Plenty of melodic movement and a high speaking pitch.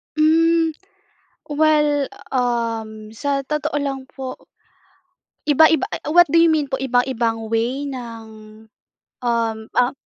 No: average, 4.4 semitones; very high, 270 Hz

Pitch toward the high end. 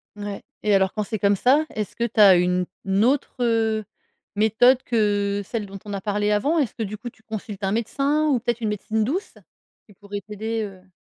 Yes: high, 215 Hz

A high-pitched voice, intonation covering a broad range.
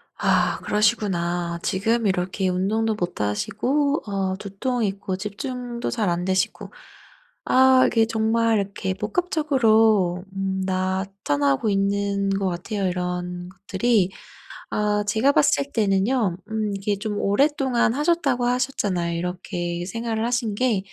No: high, 205 Hz; average, 3.7 semitones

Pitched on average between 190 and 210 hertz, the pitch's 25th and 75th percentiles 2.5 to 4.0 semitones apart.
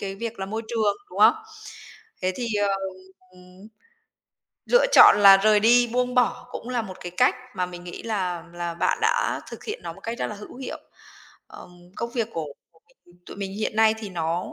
No: high, 205 Hz; average, 4.4 semitones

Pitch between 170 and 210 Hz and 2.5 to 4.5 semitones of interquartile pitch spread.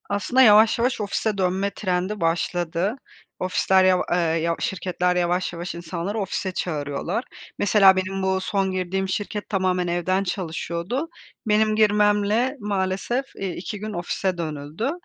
Yes: high, 190 Hz; average, 2.8 semitones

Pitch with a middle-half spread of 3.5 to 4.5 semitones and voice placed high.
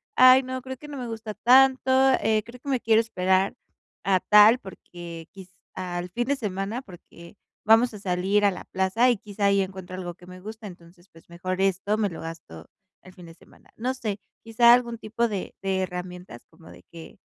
Yes: average, 4.2 semitones; high, 200 Hz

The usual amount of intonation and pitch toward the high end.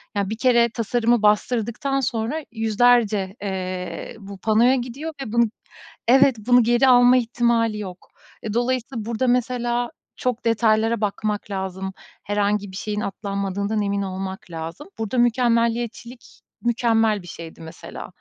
Yes: average, 3.1 semitones; high, 225 Hz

